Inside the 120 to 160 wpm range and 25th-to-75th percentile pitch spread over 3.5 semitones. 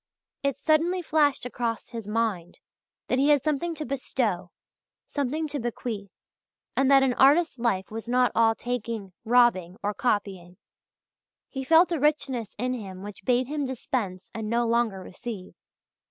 Yes: average, 155 wpm; average, 4.7 semitones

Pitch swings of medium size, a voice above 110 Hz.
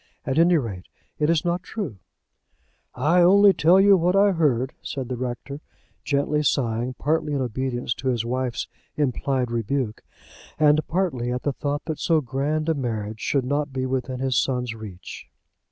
Yes: average, 4.0 semitones; low, 135 Hz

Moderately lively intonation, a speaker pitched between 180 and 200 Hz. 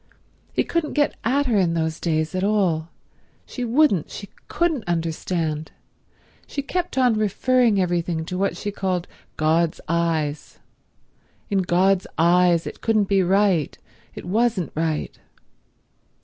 Yes: average, 4.6 semitones; medium, 185 Hz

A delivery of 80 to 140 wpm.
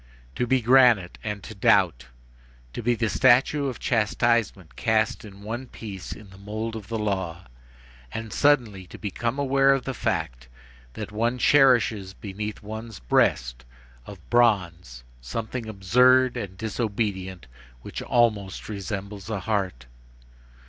Yes: slow, 135 wpm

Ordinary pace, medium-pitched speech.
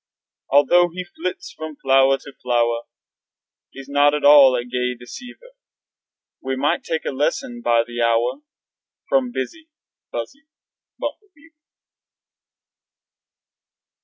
No: slow, 105 wpm; medium, 145 Hz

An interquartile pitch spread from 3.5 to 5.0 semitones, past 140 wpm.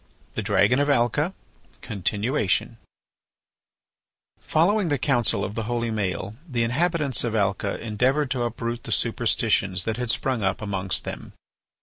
No: average, 4.2 semitones; slow, 135 wpm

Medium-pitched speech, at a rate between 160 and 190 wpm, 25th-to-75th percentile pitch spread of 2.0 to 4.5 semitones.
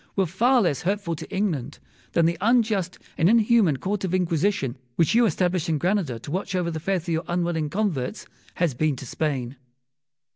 Yes: medium, 175 Hz; average, 185 wpm; average, 4.1 semitones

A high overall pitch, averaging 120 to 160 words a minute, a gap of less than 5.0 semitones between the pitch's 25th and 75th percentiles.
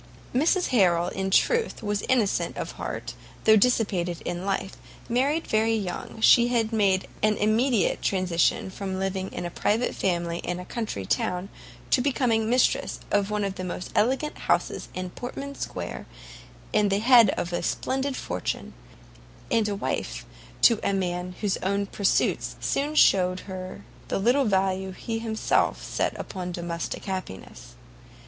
Yes: high, 200 Hz; average, 150 wpm; average, 4.1 semitones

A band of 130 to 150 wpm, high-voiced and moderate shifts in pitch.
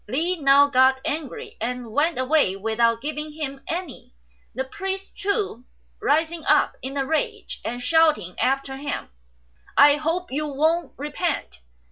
Yes: average, 140 wpm; very high, 285 Hz; average, 3.7 semitones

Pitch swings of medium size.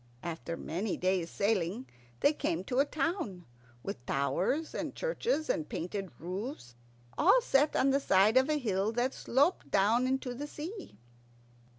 No: wide, 7.8 semitones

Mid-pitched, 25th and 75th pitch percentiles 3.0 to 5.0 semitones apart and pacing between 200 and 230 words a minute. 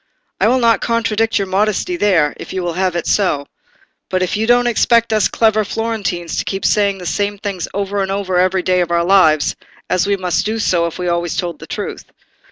No: high, 195 Hz; average, 3.3 semitones; fast, 205 wpm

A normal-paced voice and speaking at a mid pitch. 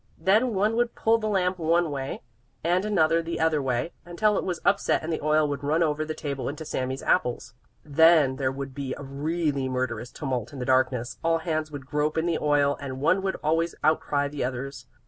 No: fast, 210 wpm; medium, 155 Hz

